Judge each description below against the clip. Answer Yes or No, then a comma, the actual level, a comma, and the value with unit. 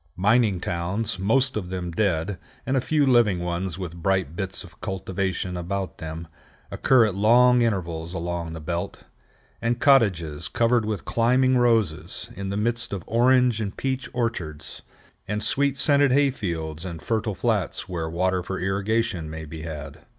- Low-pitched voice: Yes, very low, 95 Hz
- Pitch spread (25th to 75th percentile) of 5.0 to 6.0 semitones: Yes, wide, 5.4 semitones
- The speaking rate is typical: Yes, average, 160 wpm